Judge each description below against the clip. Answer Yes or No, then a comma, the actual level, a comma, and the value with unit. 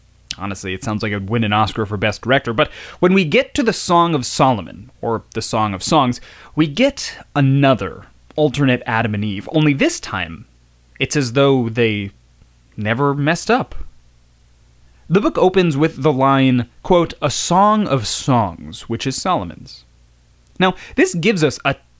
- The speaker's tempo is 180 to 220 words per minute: No, average, 165 wpm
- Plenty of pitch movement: Yes, wide, 7.3 semitones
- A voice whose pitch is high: No, low, 120 Hz